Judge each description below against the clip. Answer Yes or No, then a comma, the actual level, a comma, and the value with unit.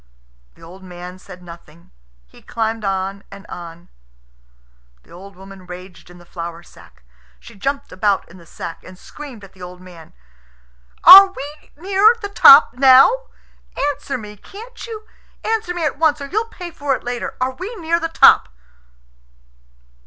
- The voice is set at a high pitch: Yes, high, 220 Hz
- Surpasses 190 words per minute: No, average, 165 wpm